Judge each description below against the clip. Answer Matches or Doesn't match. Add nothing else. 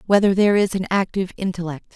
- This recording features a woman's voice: Matches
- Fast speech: Doesn't match